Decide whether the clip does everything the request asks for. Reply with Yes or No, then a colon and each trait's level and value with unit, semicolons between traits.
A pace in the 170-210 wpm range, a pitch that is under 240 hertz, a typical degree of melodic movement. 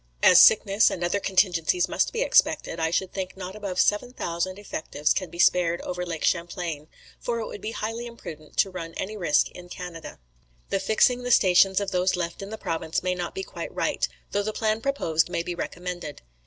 Yes: average, 200 wpm; medium, 185 Hz; average, 3.3 semitones